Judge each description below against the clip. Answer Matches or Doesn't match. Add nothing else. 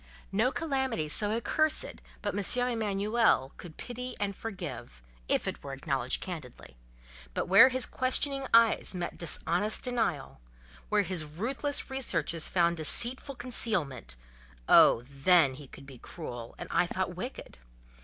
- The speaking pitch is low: Doesn't match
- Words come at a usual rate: Doesn't match